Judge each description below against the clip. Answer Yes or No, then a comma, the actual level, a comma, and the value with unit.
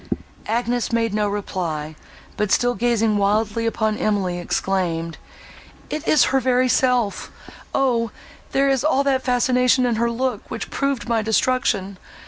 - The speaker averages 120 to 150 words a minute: Yes, average, 140 wpm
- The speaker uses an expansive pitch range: No, average, 3.6 semitones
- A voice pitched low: No, high, 230 Hz